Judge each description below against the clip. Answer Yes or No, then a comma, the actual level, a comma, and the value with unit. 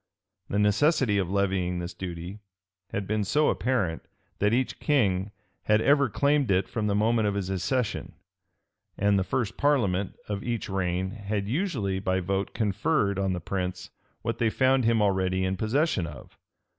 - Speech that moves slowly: No, average, 165 wpm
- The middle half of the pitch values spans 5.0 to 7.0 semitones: No, average, 3.8 semitones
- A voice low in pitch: Yes, low, 100 Hz